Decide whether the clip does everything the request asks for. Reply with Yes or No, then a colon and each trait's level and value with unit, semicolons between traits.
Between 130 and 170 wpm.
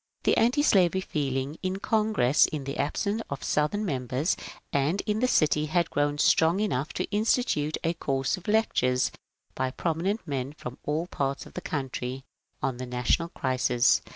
Yes: average, 160 wpm